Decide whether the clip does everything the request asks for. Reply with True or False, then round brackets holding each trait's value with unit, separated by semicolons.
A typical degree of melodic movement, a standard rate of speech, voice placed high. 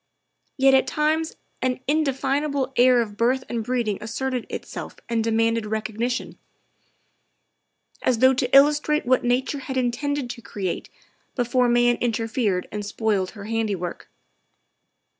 False (3.0 semitones; 125 wpm; 245 Hz)